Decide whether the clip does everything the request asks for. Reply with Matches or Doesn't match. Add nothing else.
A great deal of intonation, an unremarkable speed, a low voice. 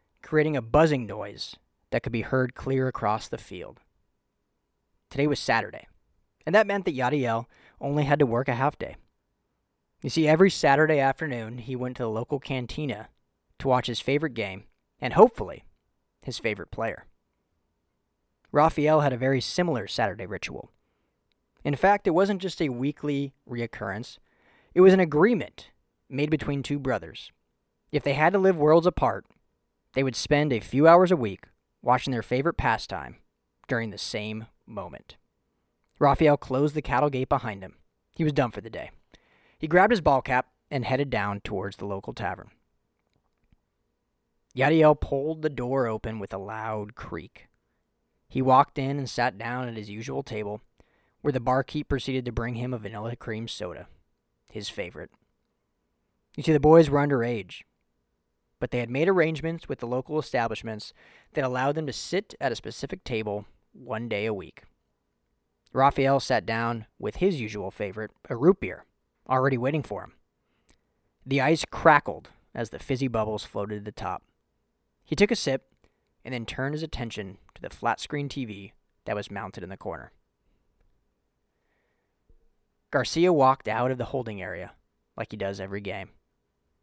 Matches